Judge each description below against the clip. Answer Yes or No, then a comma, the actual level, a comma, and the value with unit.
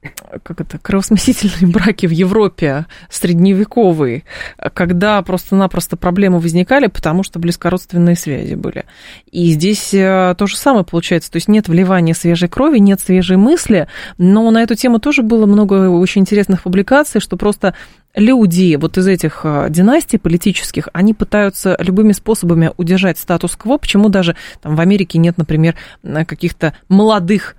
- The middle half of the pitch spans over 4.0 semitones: No, average, 3.3 semitones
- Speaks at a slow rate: No, average, 140 wpm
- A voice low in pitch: No, medium, 185 Hz